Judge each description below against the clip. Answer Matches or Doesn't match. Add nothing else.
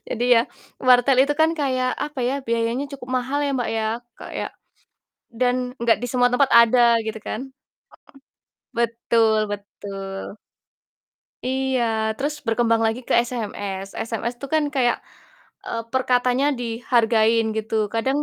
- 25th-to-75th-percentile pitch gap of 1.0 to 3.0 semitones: Matches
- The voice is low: Doesn't match